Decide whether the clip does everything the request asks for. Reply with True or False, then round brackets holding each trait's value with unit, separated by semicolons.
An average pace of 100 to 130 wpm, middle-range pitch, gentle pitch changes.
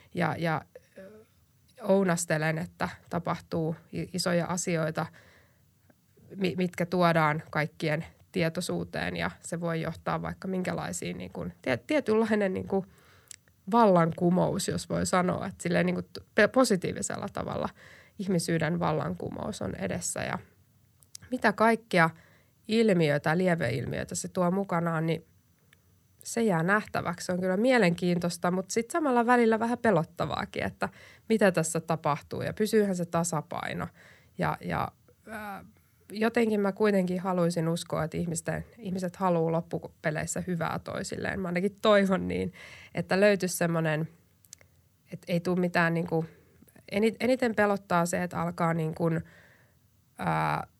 False (120 wpm; 175 Hz; 3.5 semitones)